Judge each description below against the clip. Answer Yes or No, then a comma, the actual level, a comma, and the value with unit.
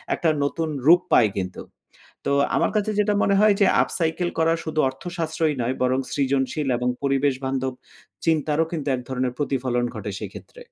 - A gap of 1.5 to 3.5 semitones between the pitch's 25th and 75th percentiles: No, average, 4.0 semitones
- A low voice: No, medium, 145 Hz